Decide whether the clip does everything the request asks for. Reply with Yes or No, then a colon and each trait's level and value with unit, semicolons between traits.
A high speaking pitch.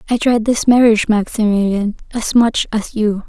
Yes: high, 220 Hz